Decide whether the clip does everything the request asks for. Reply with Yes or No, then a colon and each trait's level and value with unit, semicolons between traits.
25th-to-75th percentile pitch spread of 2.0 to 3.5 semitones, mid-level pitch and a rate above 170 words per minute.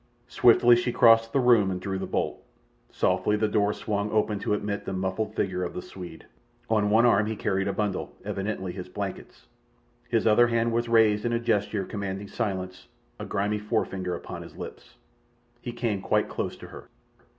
No: average, 2.8 semitones; low, 105 Hz; average, 185 wpm